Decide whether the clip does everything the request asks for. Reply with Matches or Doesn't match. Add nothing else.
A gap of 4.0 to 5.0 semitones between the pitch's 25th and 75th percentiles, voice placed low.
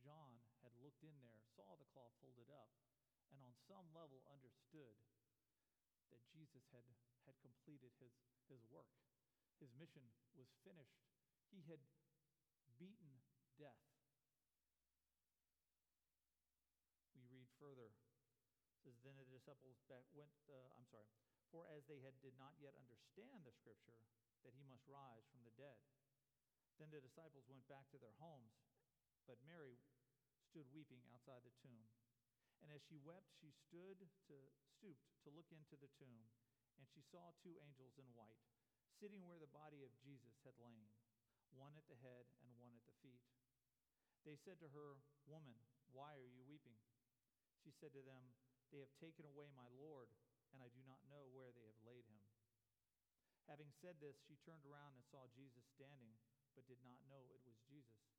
Doesn't match